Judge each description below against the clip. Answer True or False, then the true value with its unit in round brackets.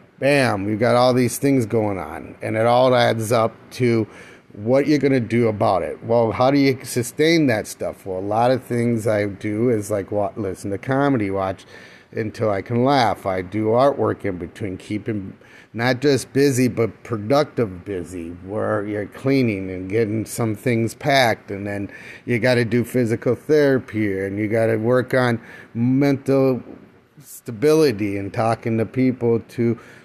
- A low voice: True (115 Hz)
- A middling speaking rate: True (170 wpm)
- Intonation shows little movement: False (3.5 semitones)